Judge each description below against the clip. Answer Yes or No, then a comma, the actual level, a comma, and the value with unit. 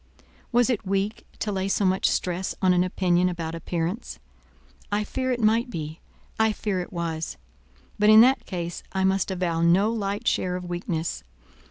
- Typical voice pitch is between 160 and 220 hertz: Yes, high, 190 Hz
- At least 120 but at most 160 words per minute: No, average, 175 wpm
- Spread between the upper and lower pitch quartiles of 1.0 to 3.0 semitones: No, average, 3.4 semitones